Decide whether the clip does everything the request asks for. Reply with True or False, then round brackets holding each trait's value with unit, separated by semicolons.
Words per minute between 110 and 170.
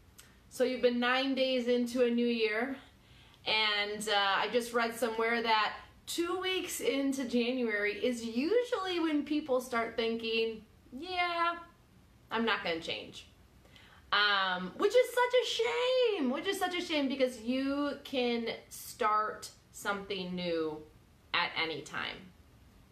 True (135 wpm)